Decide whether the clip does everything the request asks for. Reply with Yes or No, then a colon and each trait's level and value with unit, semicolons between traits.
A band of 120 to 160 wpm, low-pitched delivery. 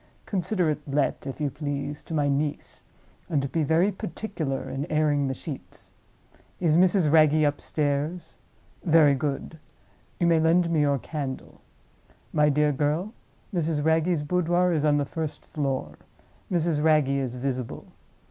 No: average, 140 wpm; medium, 150 Hz